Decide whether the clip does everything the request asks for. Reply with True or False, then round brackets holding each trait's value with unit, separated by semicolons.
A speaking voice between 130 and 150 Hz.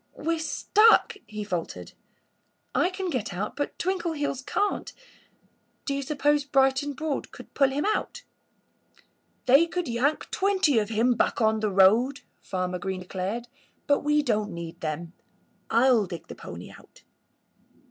False (265 Hz)